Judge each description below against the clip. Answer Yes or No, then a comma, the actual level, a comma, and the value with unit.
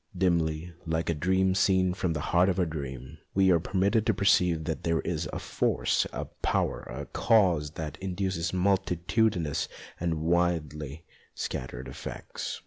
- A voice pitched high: No, very low, 85 Hz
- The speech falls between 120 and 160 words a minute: Yes, average, 150 wpm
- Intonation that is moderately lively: Yes, average, 3.0 semitones